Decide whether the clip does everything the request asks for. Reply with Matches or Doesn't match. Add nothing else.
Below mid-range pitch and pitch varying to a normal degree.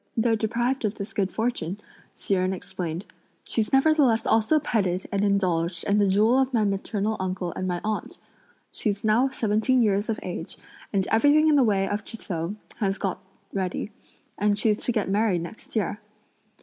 Doesn't match